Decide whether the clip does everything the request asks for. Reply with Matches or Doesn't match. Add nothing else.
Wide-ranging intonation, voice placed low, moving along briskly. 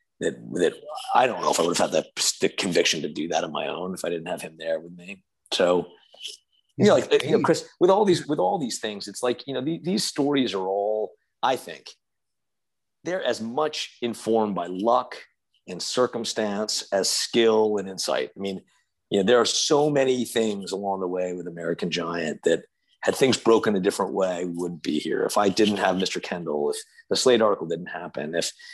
Matches